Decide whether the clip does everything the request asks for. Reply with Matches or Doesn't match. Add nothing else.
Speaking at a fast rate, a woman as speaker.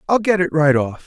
Doesn't match